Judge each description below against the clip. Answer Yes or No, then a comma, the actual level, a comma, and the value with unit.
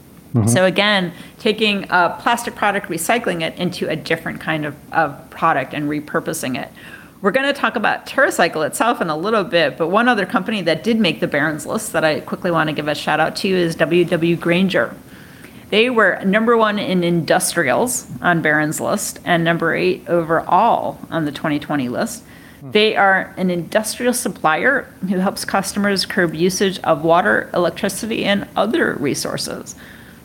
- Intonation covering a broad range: No, average, 4.5 semitones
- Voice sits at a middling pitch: Yes, medium, 180 Hz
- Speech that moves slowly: No, average, 170 wpm